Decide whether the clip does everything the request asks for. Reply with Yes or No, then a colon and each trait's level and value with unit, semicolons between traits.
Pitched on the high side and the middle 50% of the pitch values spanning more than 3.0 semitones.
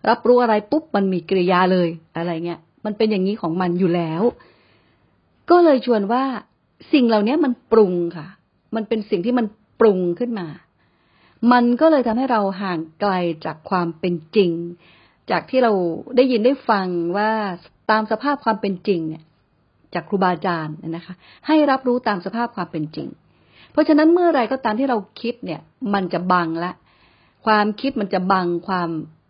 Yes: high, 205 Hz; wide, 5.5 semitones